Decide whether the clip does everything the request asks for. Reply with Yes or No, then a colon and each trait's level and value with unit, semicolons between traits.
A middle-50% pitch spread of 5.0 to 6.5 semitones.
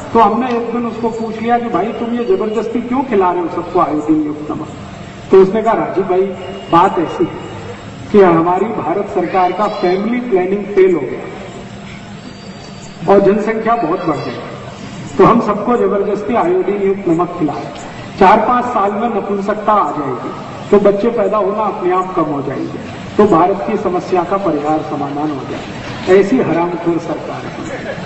No: average, 3.8 semitones